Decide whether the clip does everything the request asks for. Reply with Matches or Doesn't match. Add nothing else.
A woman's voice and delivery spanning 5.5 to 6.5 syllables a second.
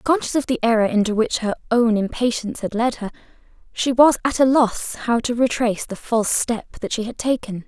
Matches